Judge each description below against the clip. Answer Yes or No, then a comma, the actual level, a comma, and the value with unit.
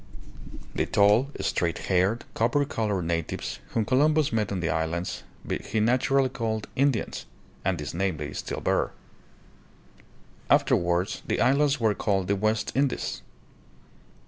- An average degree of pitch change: No, wide, 6.0 semitones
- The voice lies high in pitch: No, low, 105 Hz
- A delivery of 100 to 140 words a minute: Yes, slow, 135 wpm